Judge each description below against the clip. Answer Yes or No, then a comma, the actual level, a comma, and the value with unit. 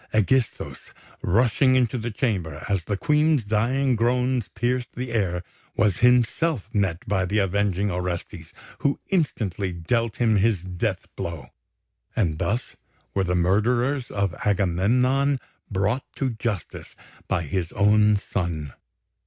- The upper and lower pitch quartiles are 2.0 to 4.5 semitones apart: No, average, 5.0 semitones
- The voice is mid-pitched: No, low, 105 Hz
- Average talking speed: No, slow, 130 wpm